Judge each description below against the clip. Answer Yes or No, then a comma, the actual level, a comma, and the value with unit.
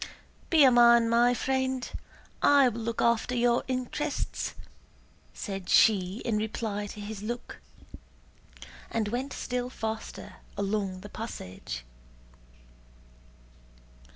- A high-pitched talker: Yes, high, 230 Hz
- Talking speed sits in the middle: No, slow, 105 wpm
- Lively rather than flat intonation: No, average, 3.1 semitones